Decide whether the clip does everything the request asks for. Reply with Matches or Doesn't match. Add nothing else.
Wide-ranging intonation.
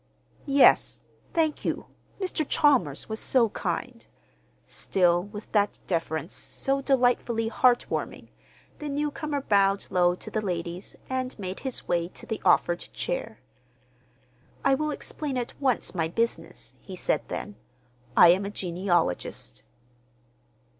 Matches